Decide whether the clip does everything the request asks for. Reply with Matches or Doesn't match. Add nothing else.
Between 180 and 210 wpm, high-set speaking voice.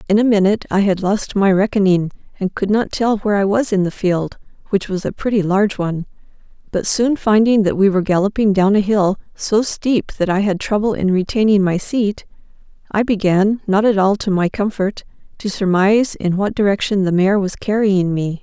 Matches